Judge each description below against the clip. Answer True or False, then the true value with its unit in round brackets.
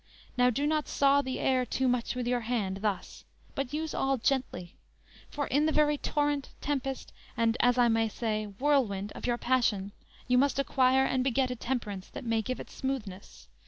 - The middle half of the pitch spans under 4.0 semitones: True (3.3 semitones)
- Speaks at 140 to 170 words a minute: False (190 wpm)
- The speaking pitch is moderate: False (250 Hz)